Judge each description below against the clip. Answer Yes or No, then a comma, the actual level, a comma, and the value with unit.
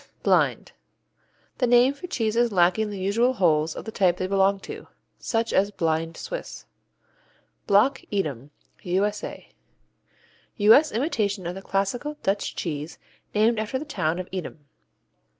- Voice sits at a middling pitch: No, high, 200 Hz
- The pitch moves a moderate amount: Yes, average, 4.5 semitones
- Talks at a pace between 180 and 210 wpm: No, slow, 135 wpm